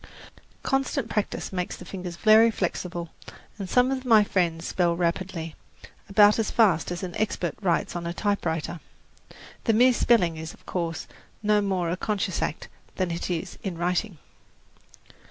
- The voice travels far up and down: No, average, 3.8 semitones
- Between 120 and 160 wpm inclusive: Yes, average, 155 wpm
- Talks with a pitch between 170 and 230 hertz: Yes, medium, 185 Hz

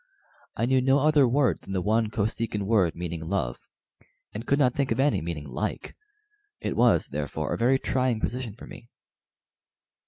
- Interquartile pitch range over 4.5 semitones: Yes, average, 5.2 semitones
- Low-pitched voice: Yes, low, 115 Hz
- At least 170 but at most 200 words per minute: Yes, average, 175 wpm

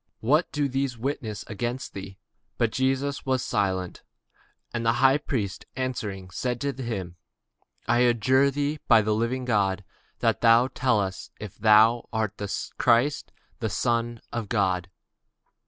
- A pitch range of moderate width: Yes, average, 3.9 semitones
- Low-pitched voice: Yes, low, 115 Hz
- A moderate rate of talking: Yes, average, 160 wpm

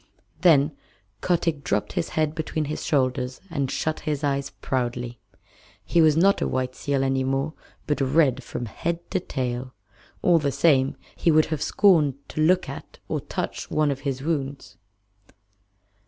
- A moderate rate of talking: Yes, average, 160 wpm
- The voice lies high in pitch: No, medium, 140 Hz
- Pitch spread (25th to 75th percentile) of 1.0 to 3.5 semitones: Yes, average, 3.2 semitones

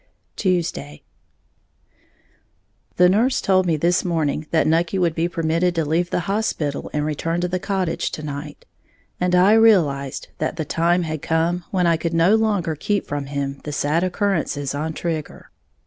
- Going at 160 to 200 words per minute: Yes, average, 165 wpm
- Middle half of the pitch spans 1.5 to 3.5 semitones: Yes, average, 3.0 semitones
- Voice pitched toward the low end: No, medium, 165 Hz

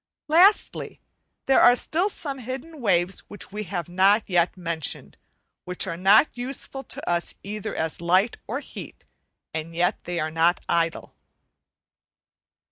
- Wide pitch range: Yes, wide, 6.6 semitones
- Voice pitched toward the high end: Yes, high, 195 Hz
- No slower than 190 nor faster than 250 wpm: No, average, 140 wpm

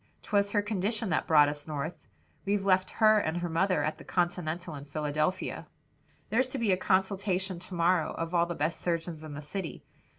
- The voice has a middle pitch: Yes, medium, 175 Hz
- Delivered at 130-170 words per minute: No, average, 195 wpm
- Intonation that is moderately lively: Yes, average, 3.8 semitones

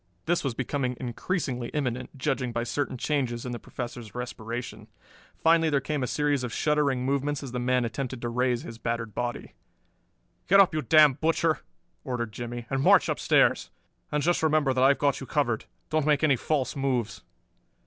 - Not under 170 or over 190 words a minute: Yes, average, 180 wpm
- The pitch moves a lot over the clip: No, average, 3.4 semitones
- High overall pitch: No, low, 130 Hz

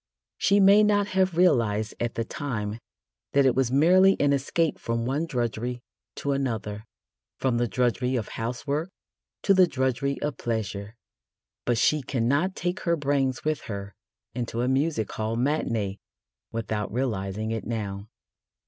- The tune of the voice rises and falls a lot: No, average, 4.7 semitones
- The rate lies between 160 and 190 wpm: No, average, 150 wpm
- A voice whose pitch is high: No, low, 125 Hz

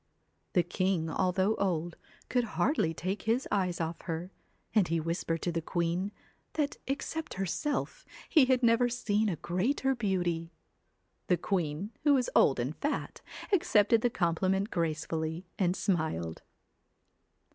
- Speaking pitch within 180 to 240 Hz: Yes, medium, 185 Hz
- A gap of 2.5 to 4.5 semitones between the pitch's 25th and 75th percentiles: No, wide, 5.5 semitones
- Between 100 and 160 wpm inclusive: Yes, slow, 135 wpm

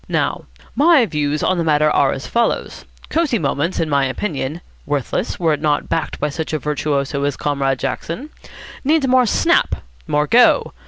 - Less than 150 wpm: No, average, 170 wpm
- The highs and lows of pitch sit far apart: Yes, wide, 6.5 semitones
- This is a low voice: No, medium, 150 Hz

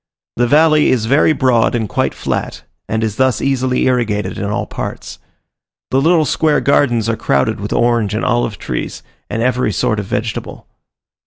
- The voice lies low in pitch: Yes, low, 120 Hz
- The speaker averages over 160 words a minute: Yes, average, 170 wpm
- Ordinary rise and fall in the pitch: Yes, average, 3.2 semitones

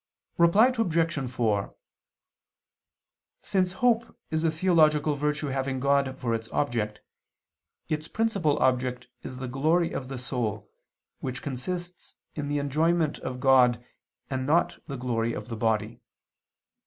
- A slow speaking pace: Yes, slow, 130 wpm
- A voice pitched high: No, medium, 140 Hz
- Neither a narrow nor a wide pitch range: Yes, average, 4.5 semitones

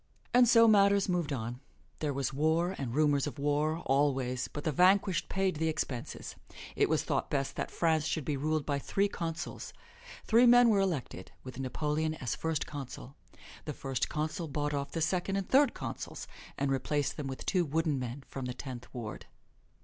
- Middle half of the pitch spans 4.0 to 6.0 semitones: Yes, average, 4.3 semitones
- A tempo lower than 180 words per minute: No, average, 185 wpm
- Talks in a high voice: No, medium, 150 Hz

